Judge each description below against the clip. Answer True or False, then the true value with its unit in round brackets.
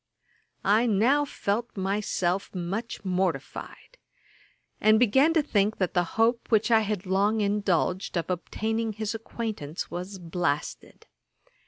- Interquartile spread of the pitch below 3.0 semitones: False (3.5 semitones)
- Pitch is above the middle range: True (205 Hz)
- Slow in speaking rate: True (125 wpm)